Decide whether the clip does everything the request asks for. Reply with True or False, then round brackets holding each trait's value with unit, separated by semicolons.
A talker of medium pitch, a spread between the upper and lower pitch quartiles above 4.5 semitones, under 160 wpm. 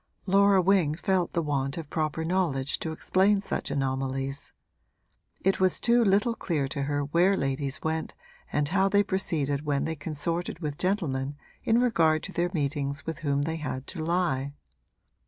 False (160 Hz; 5.0 semitones; 165 wpm)